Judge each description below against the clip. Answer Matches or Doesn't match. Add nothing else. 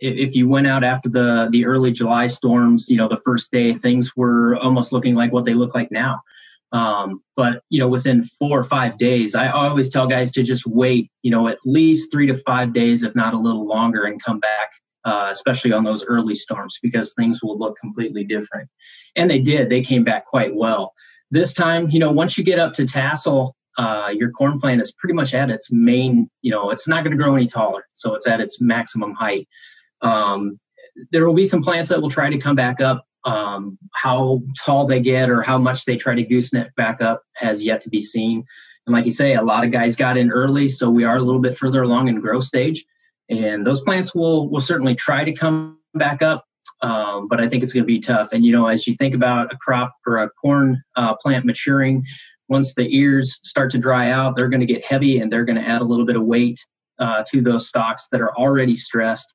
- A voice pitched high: Doesn't match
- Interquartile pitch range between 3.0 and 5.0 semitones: Doesn't match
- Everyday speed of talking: Doesn't match